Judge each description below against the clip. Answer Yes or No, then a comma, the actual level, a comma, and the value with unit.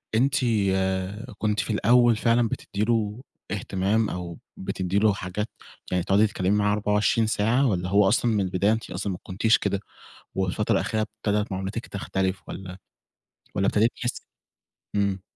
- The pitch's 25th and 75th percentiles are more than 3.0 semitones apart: No, narrow, 2.6 semitones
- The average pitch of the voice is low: Yes, low, 105 Hz